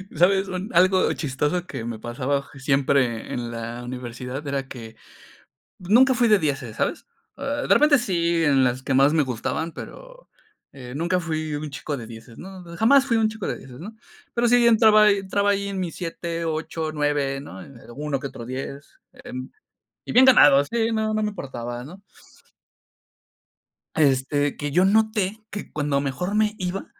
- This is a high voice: No, medium, 160 Hz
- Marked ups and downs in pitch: Yes, wide, 7.1 semitones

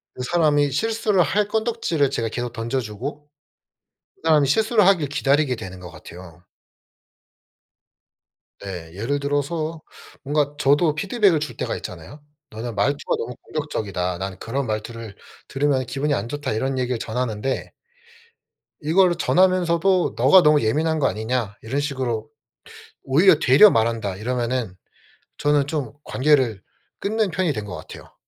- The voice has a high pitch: No, medium, 140 Hz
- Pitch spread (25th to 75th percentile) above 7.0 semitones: No, wide, 5.6 semitones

